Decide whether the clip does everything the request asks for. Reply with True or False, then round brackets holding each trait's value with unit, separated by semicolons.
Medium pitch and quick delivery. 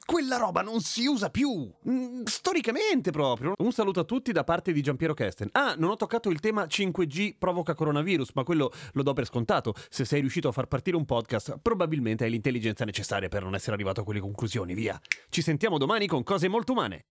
True (165 Hz; 205 wpm)